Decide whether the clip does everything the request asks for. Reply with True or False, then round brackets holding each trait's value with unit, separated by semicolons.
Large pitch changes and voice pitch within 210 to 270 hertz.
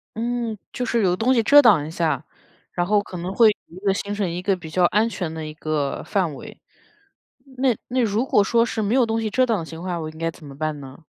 False (5.8 semitones; 195 Hz)